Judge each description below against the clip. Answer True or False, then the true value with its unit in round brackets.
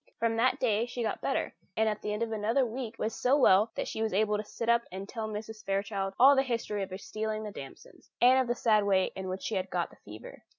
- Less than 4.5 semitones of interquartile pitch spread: True (2.8 semitones)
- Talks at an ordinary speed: False (265 wpm)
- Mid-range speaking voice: False (215 Hz)